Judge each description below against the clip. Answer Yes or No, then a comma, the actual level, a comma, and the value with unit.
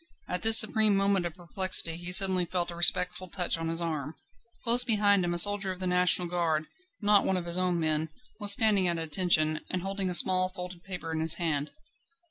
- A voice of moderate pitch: Yes, medium, 180 Hz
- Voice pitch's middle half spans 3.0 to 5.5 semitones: No, narrow, 2.5 semitones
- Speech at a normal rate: No, fast, 210 wpm